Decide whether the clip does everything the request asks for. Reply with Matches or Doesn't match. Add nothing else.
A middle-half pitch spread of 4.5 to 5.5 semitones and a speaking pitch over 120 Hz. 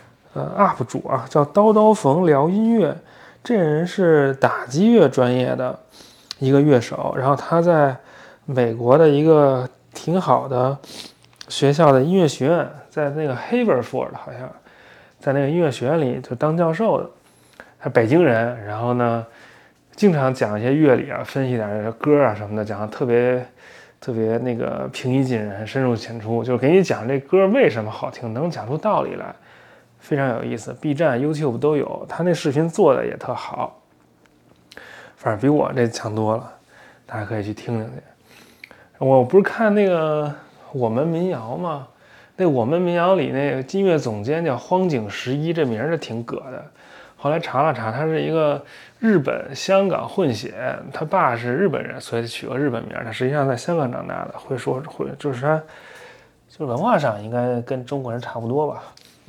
Matches